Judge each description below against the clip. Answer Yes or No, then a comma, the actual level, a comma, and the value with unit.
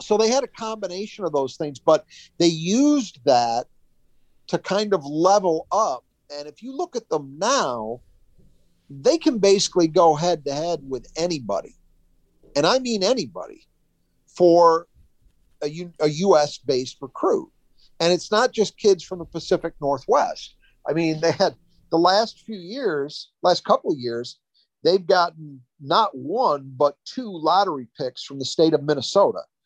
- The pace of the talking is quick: No, average, 160 wpm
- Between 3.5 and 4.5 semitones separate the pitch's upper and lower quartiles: No, average, 5.3 semitones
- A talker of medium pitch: Yes, medium, 170 Hz